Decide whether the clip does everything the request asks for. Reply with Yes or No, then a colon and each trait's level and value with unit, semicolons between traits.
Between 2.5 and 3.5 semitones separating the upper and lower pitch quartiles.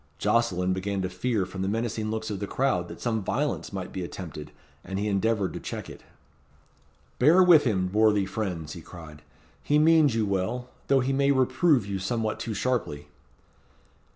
No: average, 5.1 semitones